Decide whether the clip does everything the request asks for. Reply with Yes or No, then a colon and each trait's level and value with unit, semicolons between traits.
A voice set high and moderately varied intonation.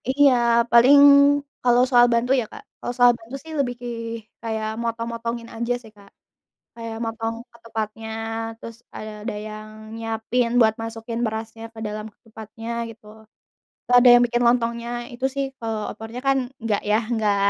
No: high, 230 Hz; narrow, 1.5 semitones